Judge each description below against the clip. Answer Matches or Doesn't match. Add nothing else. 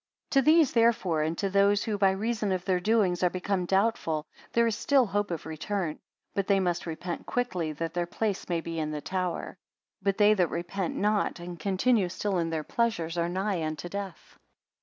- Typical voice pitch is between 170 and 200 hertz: Matches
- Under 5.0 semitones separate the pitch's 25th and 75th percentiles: Matches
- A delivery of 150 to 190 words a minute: Doesn't match